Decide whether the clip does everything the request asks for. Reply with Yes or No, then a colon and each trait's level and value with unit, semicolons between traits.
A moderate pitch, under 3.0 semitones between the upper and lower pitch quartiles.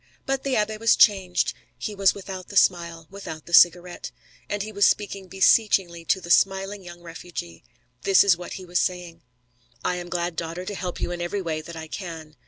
Yes: medium, 180 Hz; narrow, 2.5 semitones